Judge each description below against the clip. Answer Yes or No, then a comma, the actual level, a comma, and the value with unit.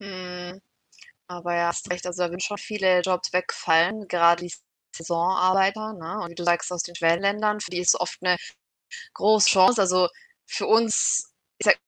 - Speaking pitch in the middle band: Yes, medium, 180 Hz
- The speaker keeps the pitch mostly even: Yes, narrow, 2.3 semitones